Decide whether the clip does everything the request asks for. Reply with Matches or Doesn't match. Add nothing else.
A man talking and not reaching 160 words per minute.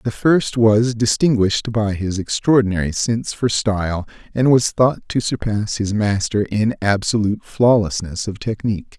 Matches